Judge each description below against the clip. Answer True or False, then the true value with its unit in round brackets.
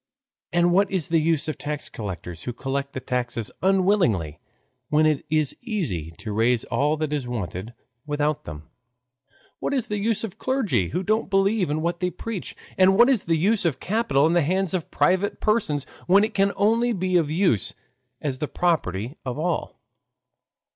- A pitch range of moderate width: False (6.9 semitones)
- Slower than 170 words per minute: False (185 wpm)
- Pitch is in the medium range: True (160 Hz)